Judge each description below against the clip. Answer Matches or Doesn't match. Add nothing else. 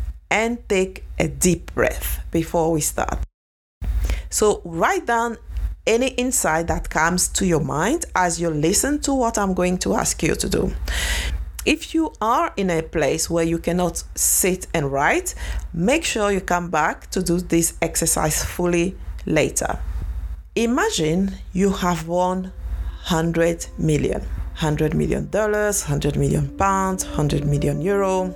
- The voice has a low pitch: Doesn't match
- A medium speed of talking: Matches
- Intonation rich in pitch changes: Doesn't match